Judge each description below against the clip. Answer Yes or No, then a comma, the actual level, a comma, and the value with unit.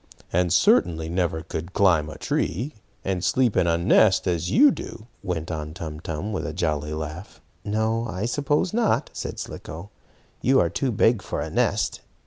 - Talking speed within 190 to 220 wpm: No, average, 180 wpm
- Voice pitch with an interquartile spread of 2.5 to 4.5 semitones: No, wide, 5.5 semitones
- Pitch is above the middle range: No, very low, 90 Hz